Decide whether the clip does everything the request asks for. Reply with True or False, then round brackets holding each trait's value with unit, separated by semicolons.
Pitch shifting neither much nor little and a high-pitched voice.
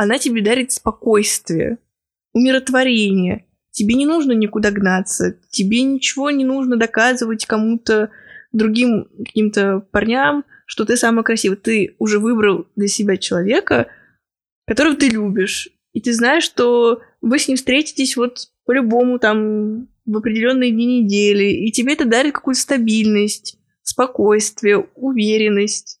True (3.2 semitones; 230 Hz)